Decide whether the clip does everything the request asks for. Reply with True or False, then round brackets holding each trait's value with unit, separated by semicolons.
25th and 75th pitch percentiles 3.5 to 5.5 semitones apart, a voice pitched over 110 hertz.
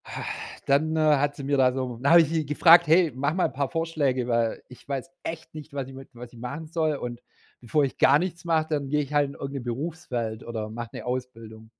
True (4.2 semitones; 140 Hz)